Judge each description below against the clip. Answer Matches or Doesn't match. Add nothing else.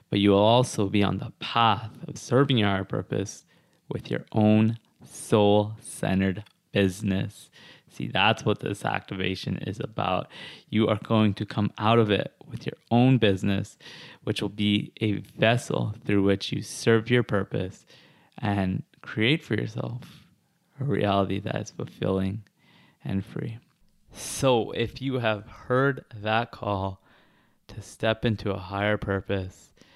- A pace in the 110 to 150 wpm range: Matches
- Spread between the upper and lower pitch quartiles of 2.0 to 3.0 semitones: Matches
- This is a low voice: Matches